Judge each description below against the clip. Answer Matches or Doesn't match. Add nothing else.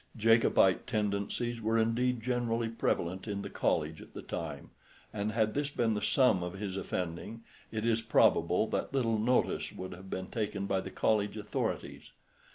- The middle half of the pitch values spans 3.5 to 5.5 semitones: Doesn't match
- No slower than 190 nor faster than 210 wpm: Doesn't match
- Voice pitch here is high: Doesn't match